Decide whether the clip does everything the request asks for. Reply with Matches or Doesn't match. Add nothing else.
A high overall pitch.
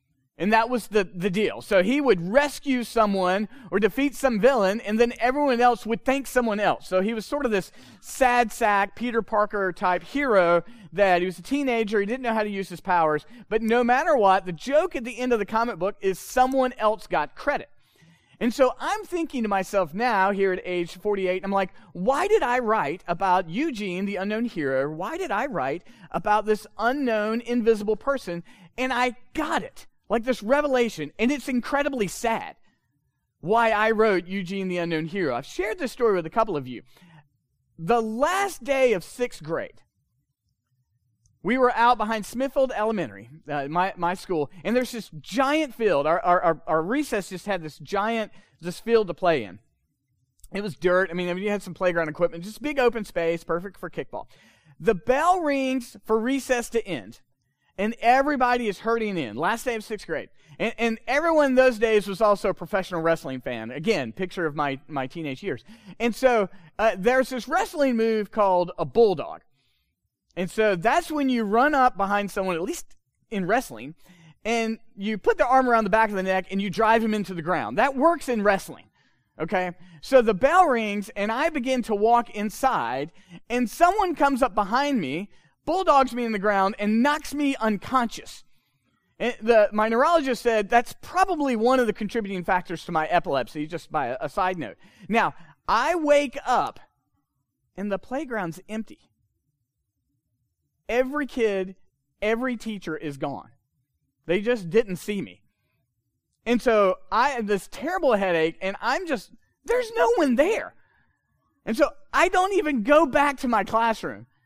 Matches